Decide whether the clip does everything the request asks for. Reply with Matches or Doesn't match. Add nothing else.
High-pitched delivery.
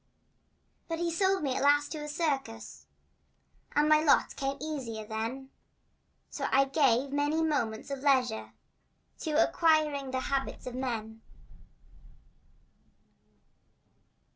Matches